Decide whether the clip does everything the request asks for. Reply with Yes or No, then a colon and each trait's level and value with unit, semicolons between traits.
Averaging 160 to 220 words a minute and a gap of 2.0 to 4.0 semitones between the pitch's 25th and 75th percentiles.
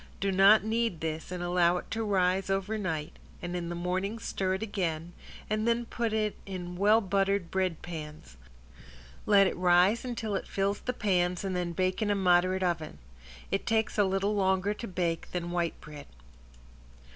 Yes: average, 180 wpm; average, 2.8 semitones